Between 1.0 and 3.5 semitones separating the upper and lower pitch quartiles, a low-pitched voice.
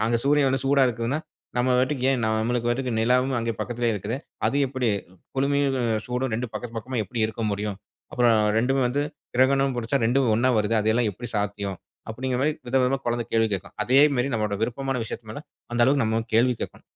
Yes: average, 2.7 semitones; low, 120 Hz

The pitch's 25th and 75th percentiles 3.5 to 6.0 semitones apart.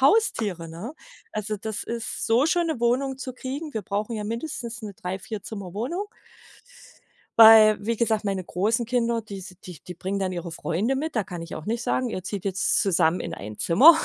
Yes: average, 4.1 semitones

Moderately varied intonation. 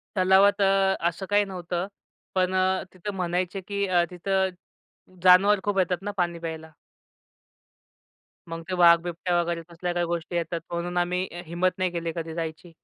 No: narrow, 1.8 semitones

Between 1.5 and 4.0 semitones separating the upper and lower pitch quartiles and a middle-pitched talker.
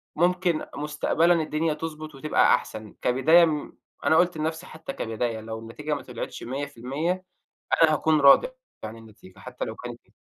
No: average, 4.6 semitones; medium, 150 Hz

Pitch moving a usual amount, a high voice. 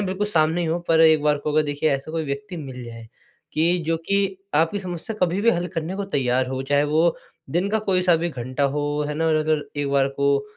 No: average, 3.6 semitones; medium, 155 Hz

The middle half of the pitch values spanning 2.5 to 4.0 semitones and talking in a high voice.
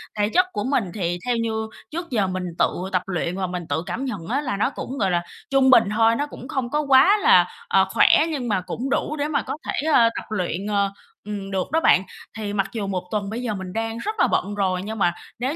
No: average, 5.3 semitones; high, 220 Hz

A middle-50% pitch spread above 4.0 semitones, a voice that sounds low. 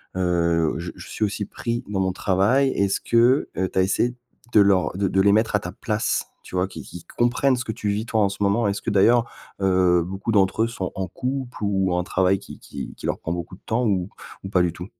No: average, 3.4 semitones; low, 100 Hz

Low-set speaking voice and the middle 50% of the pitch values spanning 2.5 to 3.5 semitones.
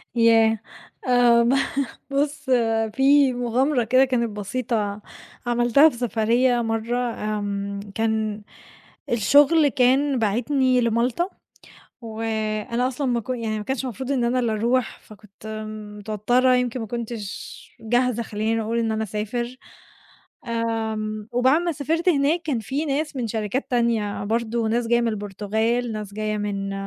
No: high, 235 Hz; average, 2.9 semitones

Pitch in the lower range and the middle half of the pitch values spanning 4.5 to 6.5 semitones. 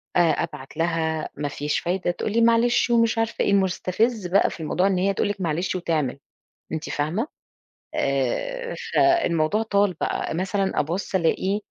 No: medium, 185 Hz; average, 5.0 semitones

